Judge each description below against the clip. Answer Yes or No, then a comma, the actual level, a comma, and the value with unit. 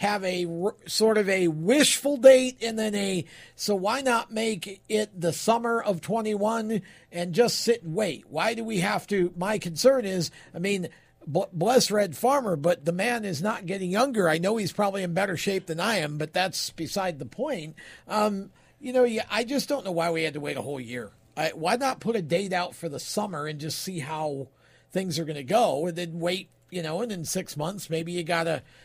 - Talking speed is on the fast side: Yes, fast, 220 wpm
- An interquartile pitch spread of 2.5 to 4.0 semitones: No, average, 4.7 semitones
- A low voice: No, high, 190 Hz